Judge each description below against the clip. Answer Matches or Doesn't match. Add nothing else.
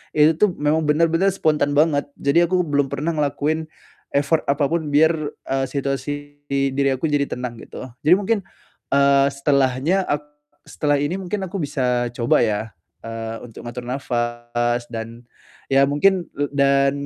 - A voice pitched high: Doesn't match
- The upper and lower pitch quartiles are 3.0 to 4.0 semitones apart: Matches